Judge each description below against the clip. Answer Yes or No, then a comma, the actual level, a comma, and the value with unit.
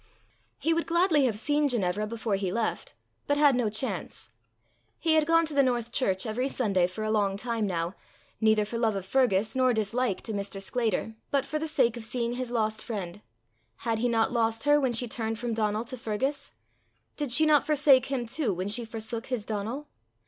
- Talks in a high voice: Yes, high, 230 Hz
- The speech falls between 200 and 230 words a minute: Yes, fast, 205 wpm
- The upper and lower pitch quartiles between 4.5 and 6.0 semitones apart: No, average, 3.8 semitones